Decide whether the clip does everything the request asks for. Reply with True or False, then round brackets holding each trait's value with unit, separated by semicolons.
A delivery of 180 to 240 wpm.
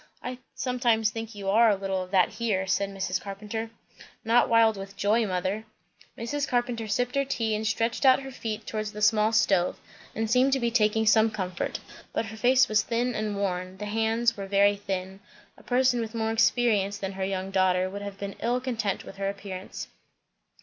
True (200 wpm)